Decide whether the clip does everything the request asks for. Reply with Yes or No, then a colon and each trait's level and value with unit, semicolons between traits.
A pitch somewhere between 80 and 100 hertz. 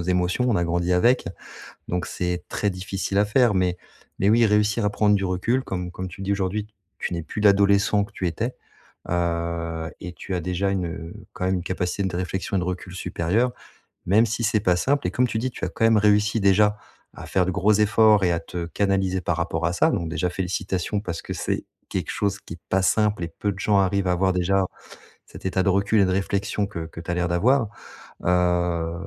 Yes: very low, 95 Hz